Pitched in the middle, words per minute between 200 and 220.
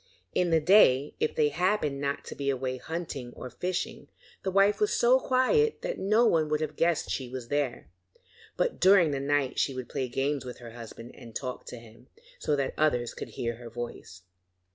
Yes: medium, 145 Hz; fast, 205 wpm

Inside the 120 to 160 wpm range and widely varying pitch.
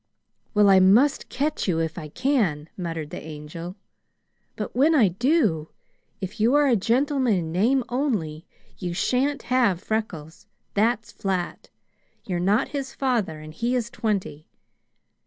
Yes: average, 145 wpm; wide, 7.1 semitones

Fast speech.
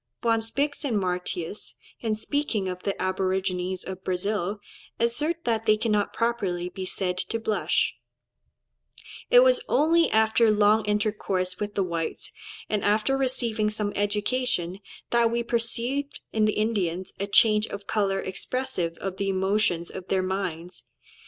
No: average, 145 wpm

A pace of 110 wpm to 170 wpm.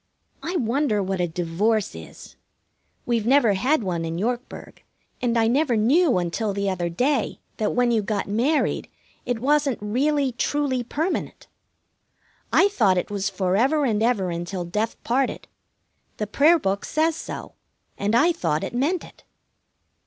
Yes: average, 160 wpm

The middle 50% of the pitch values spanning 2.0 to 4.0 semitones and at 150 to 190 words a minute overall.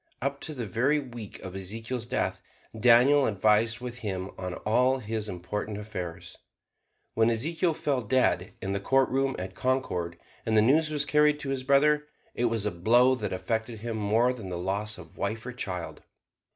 No: average, 4.4 semitones; average, 180 wpm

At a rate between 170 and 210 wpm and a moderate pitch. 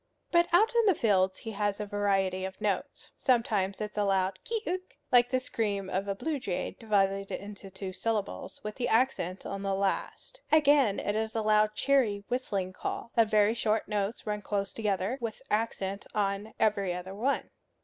No: average, 190 wpm; high, 210 Hz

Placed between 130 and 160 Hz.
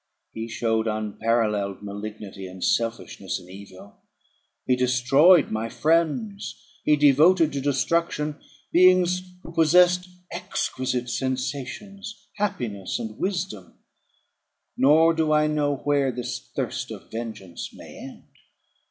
Yes: low, 135 Hz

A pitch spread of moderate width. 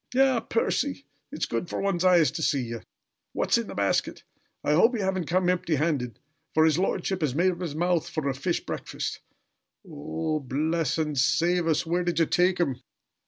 Yes: average, 3.4 semitones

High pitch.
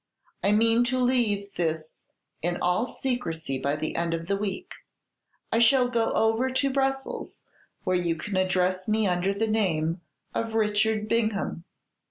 Yes: high, 210 Hz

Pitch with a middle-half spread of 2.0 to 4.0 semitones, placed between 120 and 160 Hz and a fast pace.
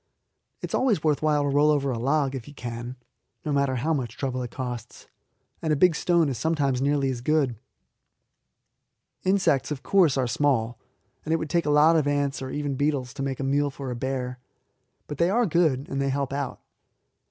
Yes: average, 2.7 semitones; medium, 140 Hz; fast, 210 wpm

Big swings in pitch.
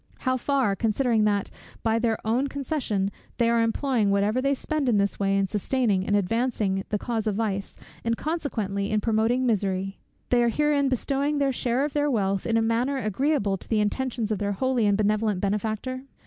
No: average, 4.2 semitones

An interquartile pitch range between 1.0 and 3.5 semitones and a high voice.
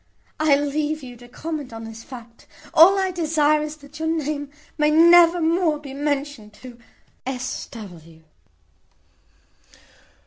No: average, 4.1 semitones; very high, 295 Hz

